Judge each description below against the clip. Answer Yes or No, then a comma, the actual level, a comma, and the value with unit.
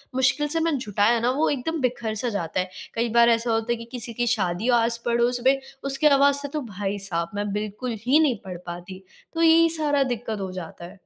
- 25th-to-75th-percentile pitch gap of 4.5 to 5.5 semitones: Yes, average, 5.0 semitones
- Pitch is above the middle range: Yes, high, 235 Hz